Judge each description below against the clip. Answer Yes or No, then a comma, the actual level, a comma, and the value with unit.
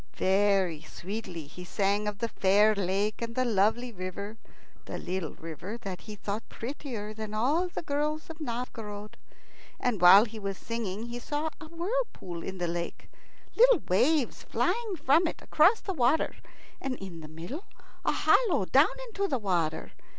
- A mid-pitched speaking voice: No, high, 215 Hz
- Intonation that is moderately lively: No, wide, 7.3 semitones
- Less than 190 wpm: Yes, average, 165 wpm